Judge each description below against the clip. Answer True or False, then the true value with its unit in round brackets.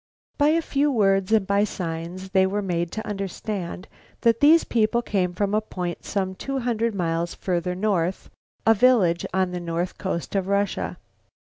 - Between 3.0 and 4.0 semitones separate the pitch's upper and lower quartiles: True (3.3 semitones)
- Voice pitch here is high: True (195 Hz)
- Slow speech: False (170 wpm)